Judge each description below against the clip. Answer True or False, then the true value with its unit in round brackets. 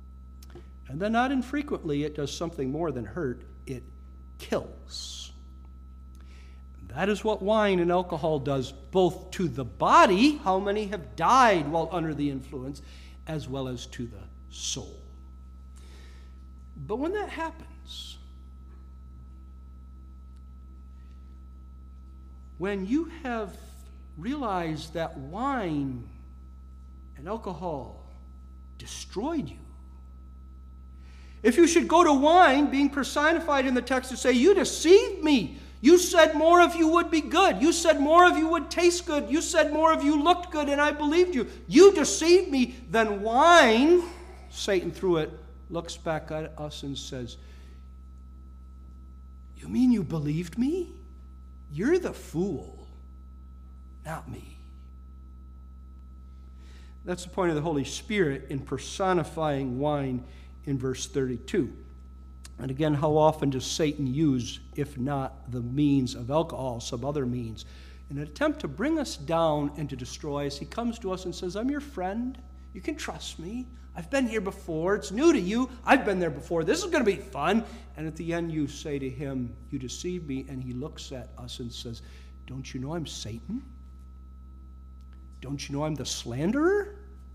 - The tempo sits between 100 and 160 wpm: True (150 wpm)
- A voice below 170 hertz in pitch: True (140 Hz)